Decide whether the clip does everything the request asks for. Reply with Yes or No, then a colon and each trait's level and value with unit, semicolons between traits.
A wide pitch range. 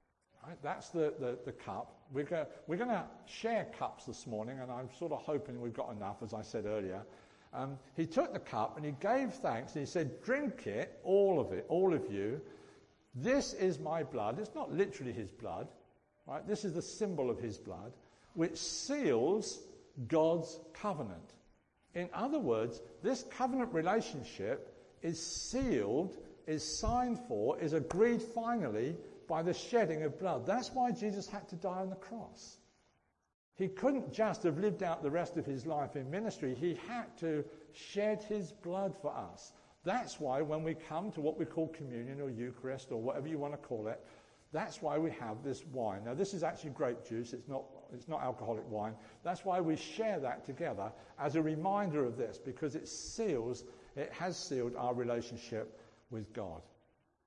Yes: wide, 7.5 semitones